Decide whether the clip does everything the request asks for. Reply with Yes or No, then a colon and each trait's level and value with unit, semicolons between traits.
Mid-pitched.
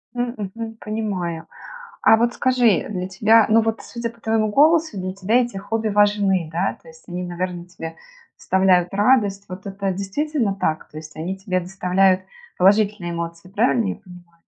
No: high, 195 Hz